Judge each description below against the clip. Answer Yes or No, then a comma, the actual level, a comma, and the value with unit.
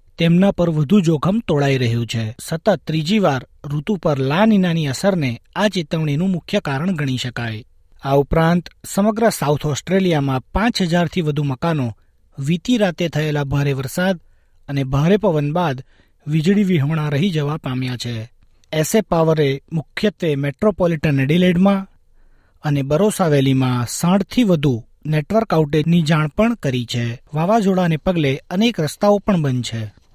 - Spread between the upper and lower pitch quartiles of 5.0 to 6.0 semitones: Yes, wide, 5.4 semitones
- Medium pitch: Yes, medium, 155 Hz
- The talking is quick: No, average, 130 wpm